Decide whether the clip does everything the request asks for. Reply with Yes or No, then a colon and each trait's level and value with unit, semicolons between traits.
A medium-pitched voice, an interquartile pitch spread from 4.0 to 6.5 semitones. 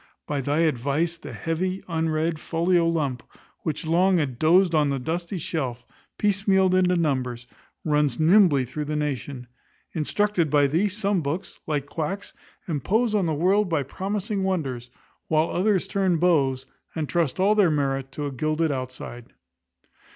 Yes: medium, 160 Hz; average, 4.5 semitones